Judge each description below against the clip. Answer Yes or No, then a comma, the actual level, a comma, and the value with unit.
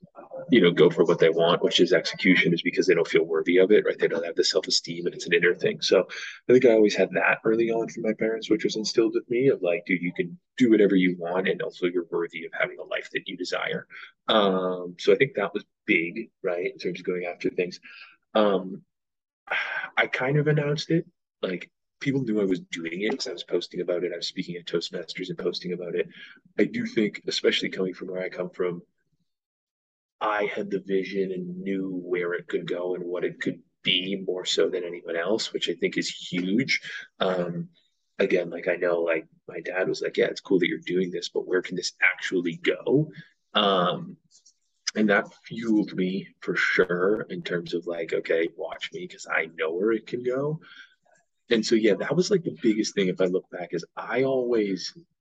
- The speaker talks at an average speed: No, fast, 220 wpm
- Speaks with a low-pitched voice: Yes, low, 125 Hz